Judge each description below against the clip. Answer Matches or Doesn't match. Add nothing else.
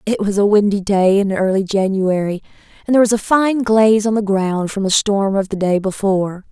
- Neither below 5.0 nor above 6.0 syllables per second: Matches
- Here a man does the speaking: Doesn't match